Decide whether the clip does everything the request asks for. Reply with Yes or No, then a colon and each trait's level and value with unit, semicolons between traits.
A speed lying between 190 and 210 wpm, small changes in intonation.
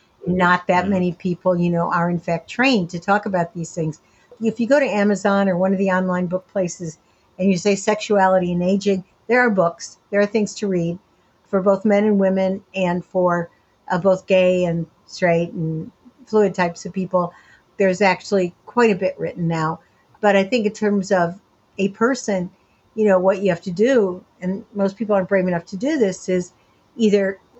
Yes: average, 200 wpm; narrow, 2.3 semitones